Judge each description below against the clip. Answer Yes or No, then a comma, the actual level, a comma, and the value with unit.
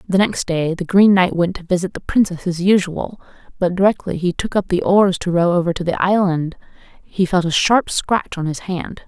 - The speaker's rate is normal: No, fast, 225 wpm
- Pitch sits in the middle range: Yes, medium, 180 Hz